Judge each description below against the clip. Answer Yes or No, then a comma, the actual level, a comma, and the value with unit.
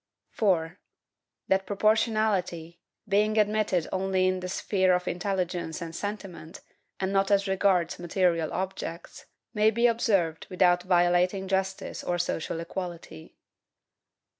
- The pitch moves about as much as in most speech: No, narrow, 2.3 semitones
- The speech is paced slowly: Yes, slow, 115 wpm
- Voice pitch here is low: No, medium, 185 Hz